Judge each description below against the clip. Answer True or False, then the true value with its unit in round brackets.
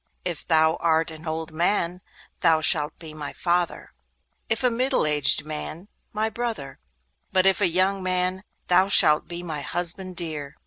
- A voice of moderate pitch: True (170 Hz)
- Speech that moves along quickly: False (165 wpm)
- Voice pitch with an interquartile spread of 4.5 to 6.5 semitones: False (2.9 semitones)